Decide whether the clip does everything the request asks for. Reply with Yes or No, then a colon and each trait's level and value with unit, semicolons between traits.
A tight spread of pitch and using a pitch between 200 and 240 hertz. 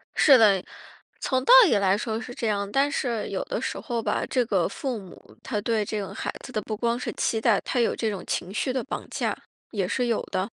No: average, 3.5 semitones; high, 225 Hz